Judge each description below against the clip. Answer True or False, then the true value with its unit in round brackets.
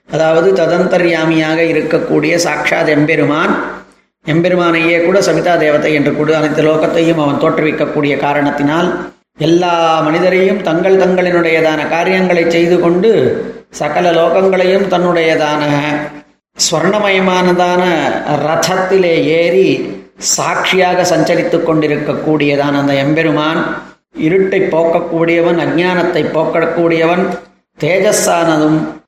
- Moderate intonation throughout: False (2.2 semitones)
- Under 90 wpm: True (75 wpm)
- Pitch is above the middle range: False (165 Hz)